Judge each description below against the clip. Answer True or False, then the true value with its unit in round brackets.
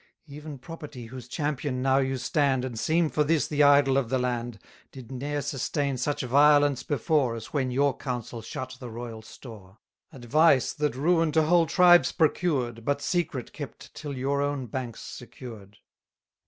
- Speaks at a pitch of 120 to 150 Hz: True (135 Hz)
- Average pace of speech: True (170 wpm)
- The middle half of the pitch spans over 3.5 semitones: False (3.1 semitones)